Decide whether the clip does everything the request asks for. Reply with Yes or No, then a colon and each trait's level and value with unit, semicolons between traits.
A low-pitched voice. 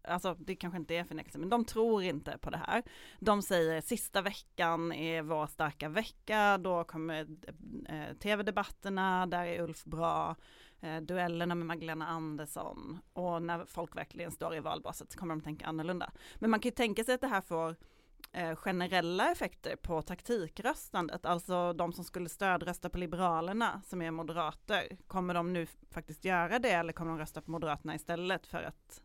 No: medium, 175 Hz